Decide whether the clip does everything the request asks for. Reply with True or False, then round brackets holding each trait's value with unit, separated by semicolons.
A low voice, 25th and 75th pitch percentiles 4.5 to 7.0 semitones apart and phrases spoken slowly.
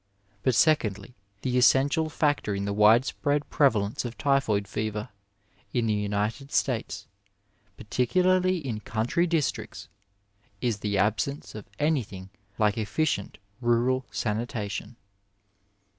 True (120 Hz; 5.1 semitones; 110 wpm)